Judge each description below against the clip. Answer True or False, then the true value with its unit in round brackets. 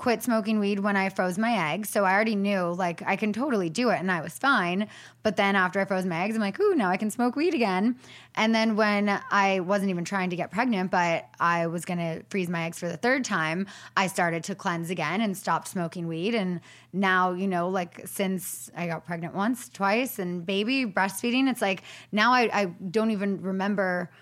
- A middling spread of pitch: True (3.5 semitones)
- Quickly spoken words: True (225 wpm)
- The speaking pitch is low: False (195 Hz)